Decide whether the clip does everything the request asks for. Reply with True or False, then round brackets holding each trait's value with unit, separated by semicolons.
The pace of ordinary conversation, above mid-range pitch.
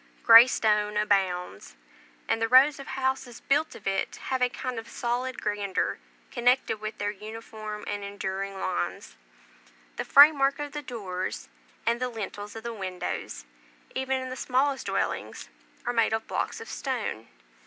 True (160 wpm; 225 Hz)